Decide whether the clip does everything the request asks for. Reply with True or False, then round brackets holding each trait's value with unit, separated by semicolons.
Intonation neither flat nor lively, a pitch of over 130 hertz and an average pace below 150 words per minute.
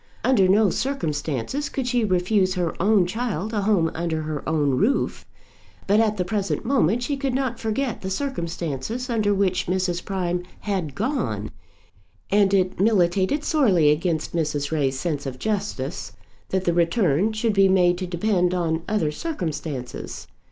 False (5.0 semitones; 185 Hz; 155 wpm)